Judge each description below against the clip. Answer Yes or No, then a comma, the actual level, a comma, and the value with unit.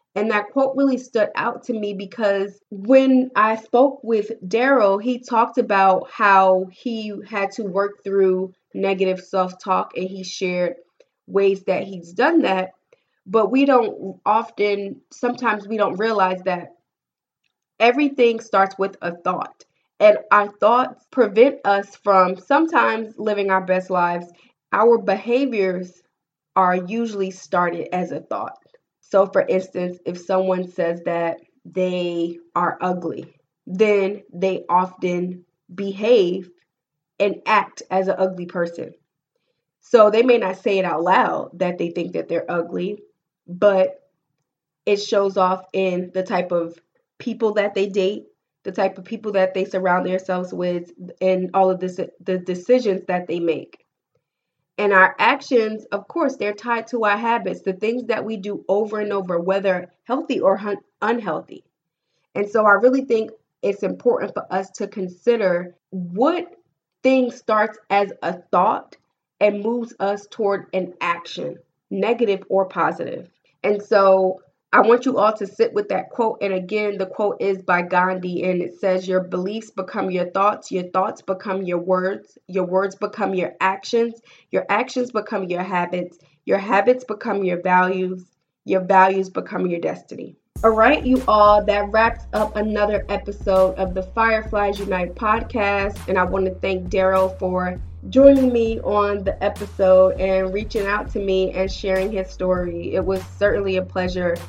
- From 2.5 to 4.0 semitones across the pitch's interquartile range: Yes, average, 2.9 semitones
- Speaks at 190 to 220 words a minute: No, average, 155 wpm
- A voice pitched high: Yes, high, 195 Hz